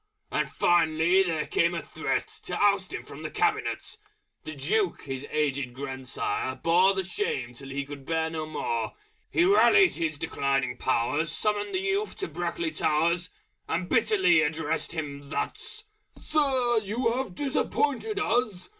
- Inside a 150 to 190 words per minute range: Yes, average, 155 wpm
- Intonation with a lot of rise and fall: Yes, wide, 8.1 semitones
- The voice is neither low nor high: Yes, medium, 170 Hz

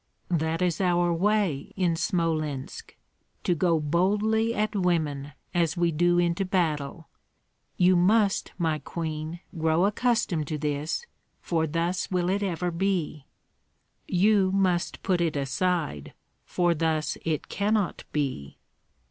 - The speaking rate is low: Yes, slow, 125 wpm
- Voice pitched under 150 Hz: No, medium, 170 Hz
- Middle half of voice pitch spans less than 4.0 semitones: Yes, average, 3.1 semitones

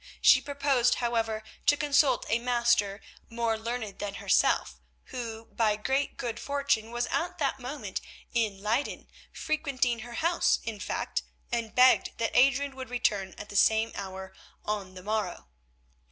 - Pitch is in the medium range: No, high, 235 Hz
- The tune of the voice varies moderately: Yes, average, 3.7 semitones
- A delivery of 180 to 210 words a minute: No, average, 150 wpm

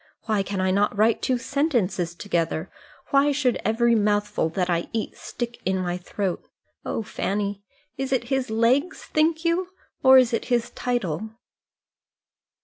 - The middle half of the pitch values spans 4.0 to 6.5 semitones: Yes, average, 5.2 semitones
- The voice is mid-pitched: No, high, 220 Hz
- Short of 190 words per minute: Yes, average, 150 wpm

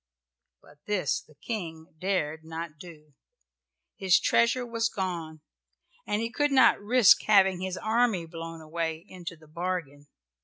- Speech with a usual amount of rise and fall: Yes, average, 4.5 semitones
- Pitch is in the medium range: Yes, medium, 175 Hz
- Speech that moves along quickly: No, average, 140 wpm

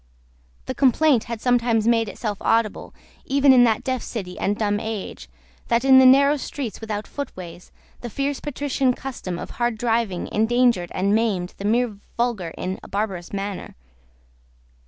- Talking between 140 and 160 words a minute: Yes, average, 155 wpm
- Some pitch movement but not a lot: Yes, average, 3.8 semitones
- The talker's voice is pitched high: Yes, high, 230 Hz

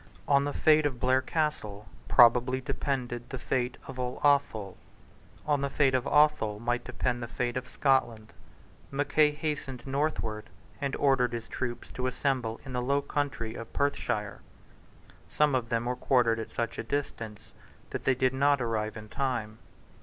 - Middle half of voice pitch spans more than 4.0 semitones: No, average, 3.2 semitones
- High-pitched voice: No, low, 125 Hz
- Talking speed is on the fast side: No, average, 165 wpm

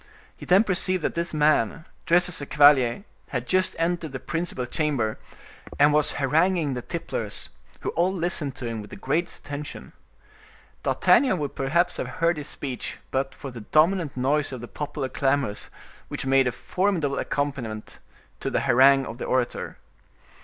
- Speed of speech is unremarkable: Yes, average, 165 wpm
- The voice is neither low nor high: Yes, medium, 145 Hz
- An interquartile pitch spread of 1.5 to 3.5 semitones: No, average, 4.4 semitones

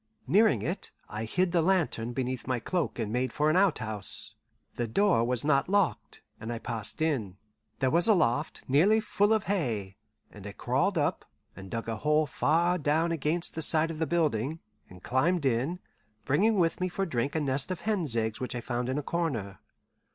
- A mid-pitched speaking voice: Yes, medium, 145 Hz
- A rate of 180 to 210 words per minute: Yes, average, 195 wpm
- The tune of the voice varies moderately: No, wide, 6.6 semitones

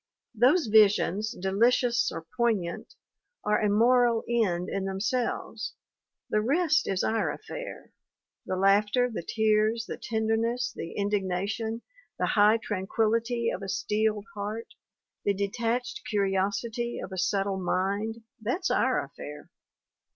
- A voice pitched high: Yes, high, 215 Hz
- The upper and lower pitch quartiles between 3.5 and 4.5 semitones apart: No, average, 2.8 semitones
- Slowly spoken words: Yes, slow, 130 wpm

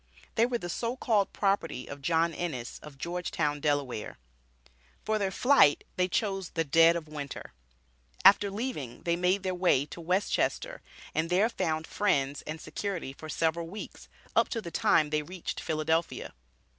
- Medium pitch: Yes, medium, 170 Hz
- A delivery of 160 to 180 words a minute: Yes, average, 165 wpm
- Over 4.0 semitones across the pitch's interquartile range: Yes, average, 4.4 semitones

